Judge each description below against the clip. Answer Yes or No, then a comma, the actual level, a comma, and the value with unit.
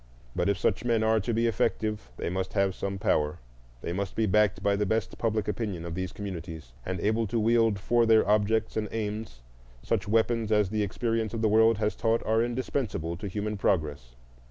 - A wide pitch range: No, average, 3.2 semitones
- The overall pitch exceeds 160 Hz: No, low, 105 Hz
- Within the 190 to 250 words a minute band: Yes, average, 200 wpm